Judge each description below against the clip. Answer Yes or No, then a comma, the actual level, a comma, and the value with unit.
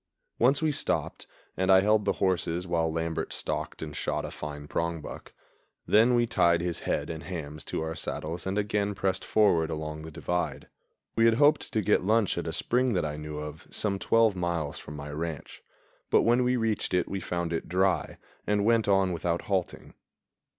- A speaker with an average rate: Yes, average, 190 wpm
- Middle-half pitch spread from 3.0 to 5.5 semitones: Yes, average, 4.5 semitones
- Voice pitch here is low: Yes, very low, 90 Hz